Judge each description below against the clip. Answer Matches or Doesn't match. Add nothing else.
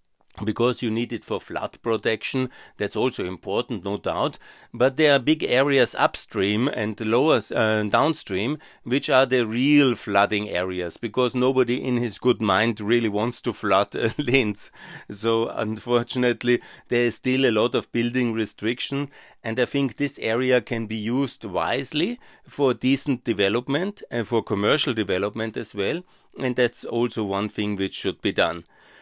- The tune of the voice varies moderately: Matches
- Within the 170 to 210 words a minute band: Doesn't match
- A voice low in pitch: Matches